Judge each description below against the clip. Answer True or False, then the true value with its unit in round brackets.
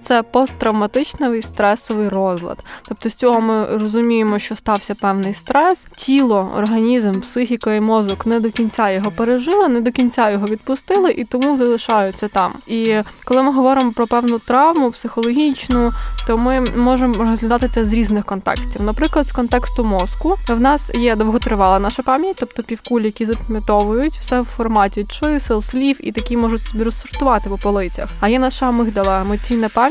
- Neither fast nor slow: False (160 wpm)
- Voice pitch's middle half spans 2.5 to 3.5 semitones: True (3.0 semitones)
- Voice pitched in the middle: False (230 Hz)